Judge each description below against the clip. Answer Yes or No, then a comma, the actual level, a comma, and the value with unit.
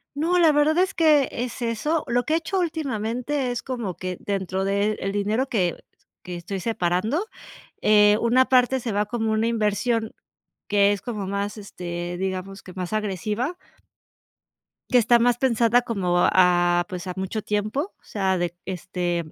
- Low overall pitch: No, high, 215 Hz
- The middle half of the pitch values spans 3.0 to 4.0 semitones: No, average, 4.6 semitones